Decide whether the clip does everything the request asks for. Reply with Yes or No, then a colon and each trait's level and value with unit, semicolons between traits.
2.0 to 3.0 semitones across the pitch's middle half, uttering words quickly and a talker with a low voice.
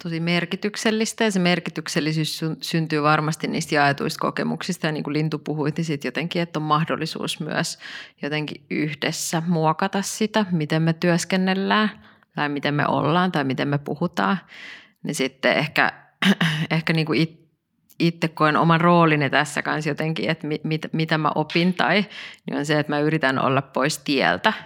No: average, 2.7 semitones; fast, 160 wpm; medium, 160 Hz